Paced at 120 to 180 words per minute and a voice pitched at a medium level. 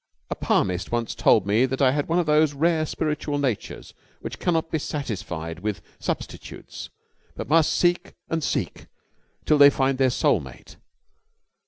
Yes: average, 160 wpm; medium, 145 Hz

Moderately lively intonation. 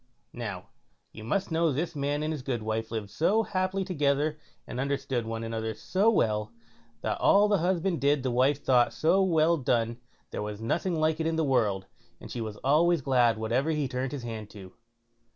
No: wide, 6.2 semitones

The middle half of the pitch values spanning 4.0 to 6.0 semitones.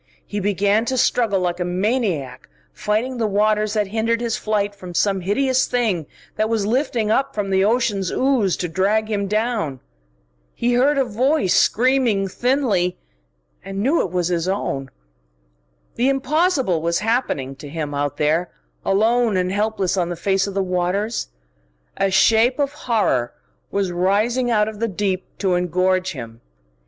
Yes: average, 4.3 semitones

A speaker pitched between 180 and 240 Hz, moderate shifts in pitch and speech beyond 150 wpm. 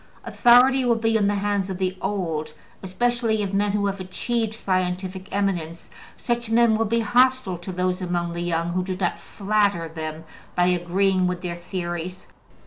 Yes: high, 190 Hz; average, 3.5 semitones; average, 175 wpm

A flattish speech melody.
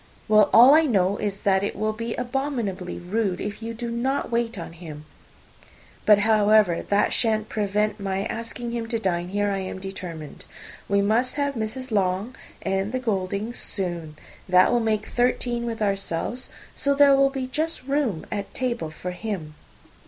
No: average, 3.7 semitones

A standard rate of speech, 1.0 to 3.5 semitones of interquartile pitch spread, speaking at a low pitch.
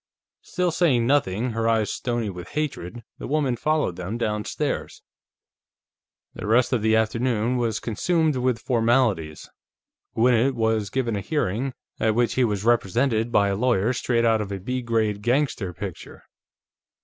Yes: average, 150 wpm; average, 3.1 semitones; low, 115 Hz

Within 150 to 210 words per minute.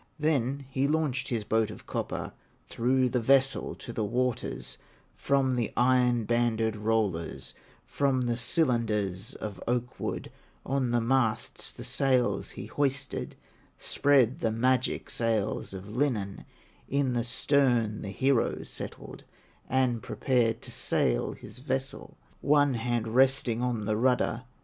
No: slow, 135 wpm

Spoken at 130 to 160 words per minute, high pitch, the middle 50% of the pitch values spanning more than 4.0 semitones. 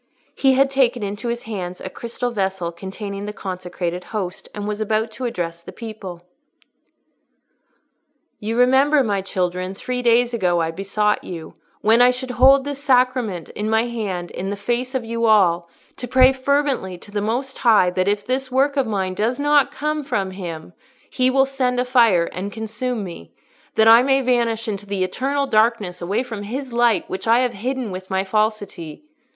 No: average, 185 wpm; high, 220 Hz; average, 4.9 semitones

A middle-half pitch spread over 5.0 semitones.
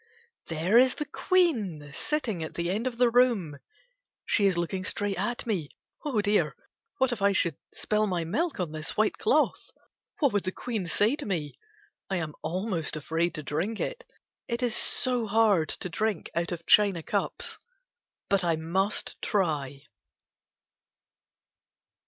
Yes: wide, 5.5 semitones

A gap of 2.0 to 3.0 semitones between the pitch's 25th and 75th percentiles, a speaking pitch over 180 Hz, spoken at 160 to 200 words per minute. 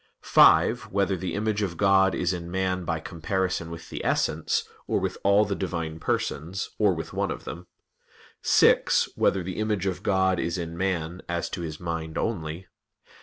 No: narrow, 2.4 semitones; very low, 90 Hz; average, 175 wpm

